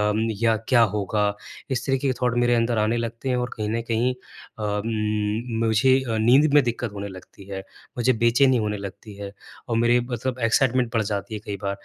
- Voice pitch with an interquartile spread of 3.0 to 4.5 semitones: No, narrow, 2.6 semitones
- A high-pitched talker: No, low, 115 Hz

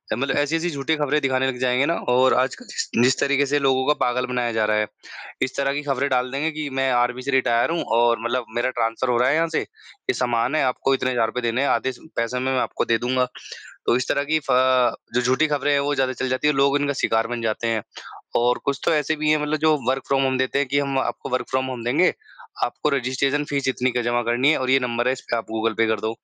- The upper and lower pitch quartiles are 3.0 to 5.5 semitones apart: No, narrow, 2.5 semitones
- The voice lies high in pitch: No, low, 130 Hz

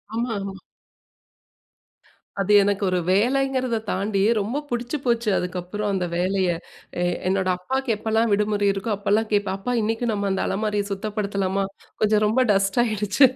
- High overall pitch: Yes, high, 205 Hz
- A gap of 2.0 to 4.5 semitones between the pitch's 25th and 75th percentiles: Yes, narrow, 2.5 semitones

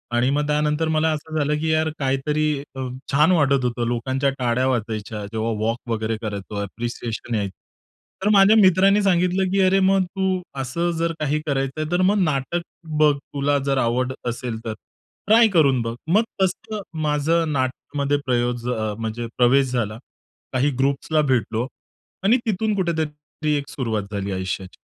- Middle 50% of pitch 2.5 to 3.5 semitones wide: No, average, 5.3 semitones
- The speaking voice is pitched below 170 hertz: Yes, medium, 140 Hz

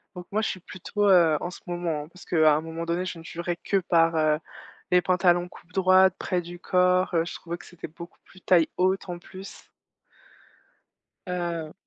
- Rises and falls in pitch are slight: Yes, narrow, 1.7 semitones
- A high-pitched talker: No, medium, 175 Hz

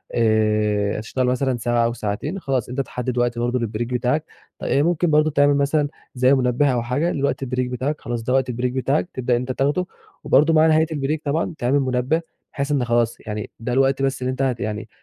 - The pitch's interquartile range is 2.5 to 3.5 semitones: Yes, average, 3.1 semitones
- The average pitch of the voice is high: No, low, 130 Hz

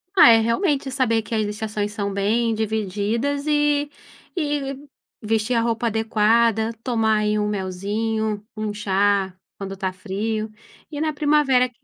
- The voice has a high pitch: Yes, high, 220 Hz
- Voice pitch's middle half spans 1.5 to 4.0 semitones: Yes, average, 3.3 semitones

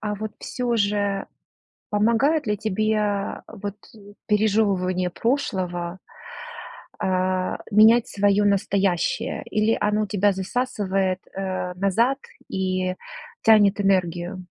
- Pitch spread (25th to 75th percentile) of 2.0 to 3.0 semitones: Yes, narrow, 2.4 semitones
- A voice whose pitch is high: Yes, high, 205 Hz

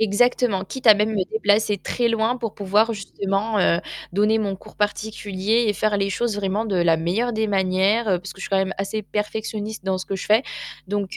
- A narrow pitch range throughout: Yes, narrow, 2.2 semitones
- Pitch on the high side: Yes, high, 205 Hz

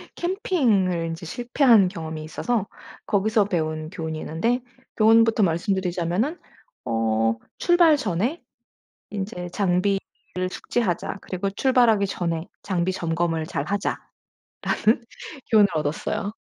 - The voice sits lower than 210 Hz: Yes, high, 190 Hz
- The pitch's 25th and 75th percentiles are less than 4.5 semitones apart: No, average, 5.2 semitones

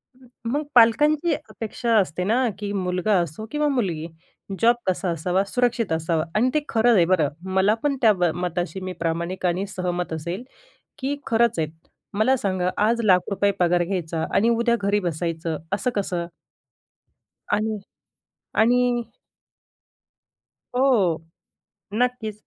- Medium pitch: No, high, 200 Hz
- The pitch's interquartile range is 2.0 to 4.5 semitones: No, average, 5.0 semitones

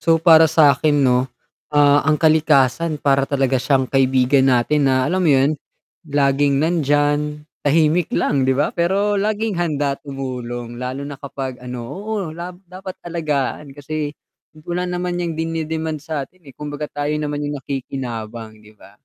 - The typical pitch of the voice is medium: Yes, medium, 145 Hz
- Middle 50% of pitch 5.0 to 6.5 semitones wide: No, average, 3.3 semitones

